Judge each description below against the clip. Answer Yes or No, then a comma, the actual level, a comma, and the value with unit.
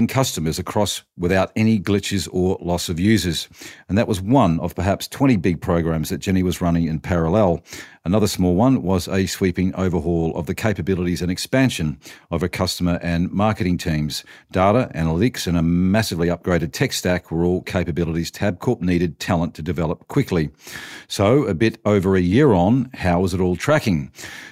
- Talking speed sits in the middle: Yes, average, 175 wpm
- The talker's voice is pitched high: No, very low, 90 Hz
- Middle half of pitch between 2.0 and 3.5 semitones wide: Yes, average, 2.7 semitones